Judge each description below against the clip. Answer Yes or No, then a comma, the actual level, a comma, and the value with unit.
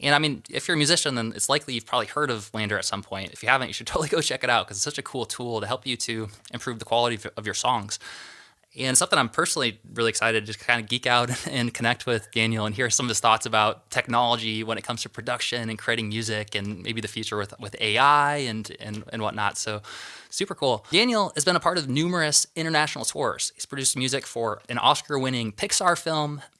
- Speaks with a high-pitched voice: No, low, 120 Hz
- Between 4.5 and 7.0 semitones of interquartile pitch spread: No, average, 3.8 semitones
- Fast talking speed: Yes, fast, 240 wpm